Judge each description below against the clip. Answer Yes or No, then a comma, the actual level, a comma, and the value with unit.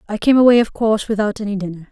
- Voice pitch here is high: Yes, high, 215 Hz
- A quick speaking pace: Yes, fast, 250 wpm